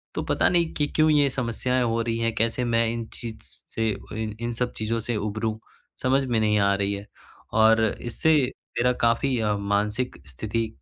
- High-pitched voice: No, low, 115 Hz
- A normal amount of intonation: No, narrow, 2.3 semitones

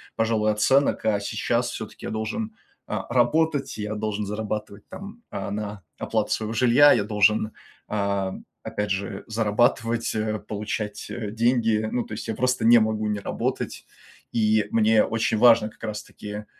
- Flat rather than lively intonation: Yes, narrow, 1.7 semitones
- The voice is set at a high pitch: No, low, 110 Hz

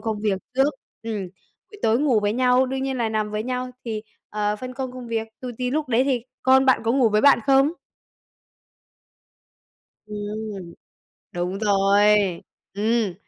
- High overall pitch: Yes, high, 230 Hz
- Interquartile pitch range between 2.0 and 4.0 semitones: Yes, average, 3.5 semitones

